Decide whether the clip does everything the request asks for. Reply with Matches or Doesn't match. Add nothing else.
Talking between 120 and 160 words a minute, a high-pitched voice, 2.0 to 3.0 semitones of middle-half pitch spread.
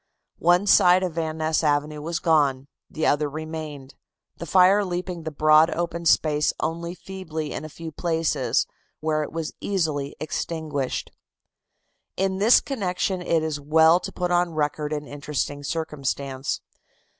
Doesn't match